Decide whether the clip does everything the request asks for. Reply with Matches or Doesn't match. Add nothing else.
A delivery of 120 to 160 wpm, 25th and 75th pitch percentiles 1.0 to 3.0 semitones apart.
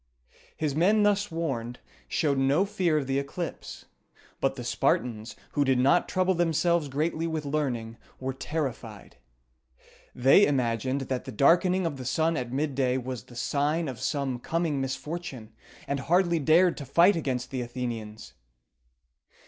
Doesn't match